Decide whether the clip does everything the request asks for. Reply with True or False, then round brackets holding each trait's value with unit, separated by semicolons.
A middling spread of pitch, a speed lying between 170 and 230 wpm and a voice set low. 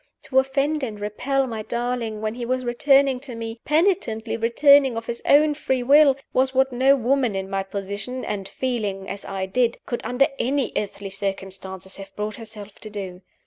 False (4.5 semitones; 185 wpm; 235 Hz)